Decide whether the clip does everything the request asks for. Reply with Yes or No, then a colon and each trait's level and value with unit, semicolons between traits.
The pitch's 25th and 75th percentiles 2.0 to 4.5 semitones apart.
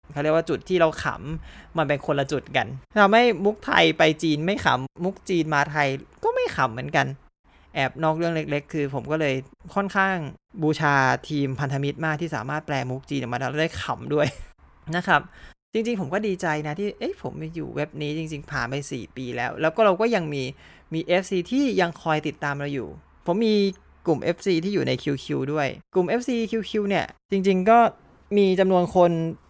No: average, 5.0 semitones